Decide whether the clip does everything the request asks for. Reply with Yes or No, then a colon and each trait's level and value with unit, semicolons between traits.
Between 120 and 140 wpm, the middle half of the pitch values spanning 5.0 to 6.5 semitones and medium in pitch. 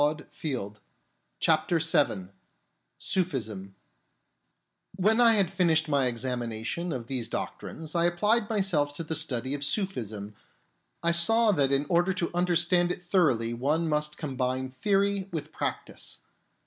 Yes: slow, 135 wpm; wide, 5.5 semitones; medium, 155 Hz